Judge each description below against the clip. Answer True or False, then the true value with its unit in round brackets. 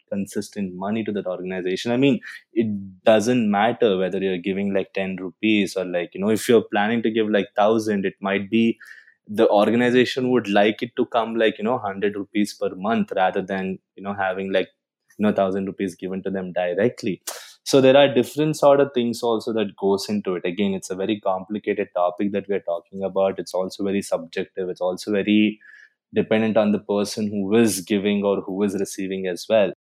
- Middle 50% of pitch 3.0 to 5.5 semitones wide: False (2.6 semitones)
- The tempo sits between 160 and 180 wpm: False (200 wpm)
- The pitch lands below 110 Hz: True (100 Hz)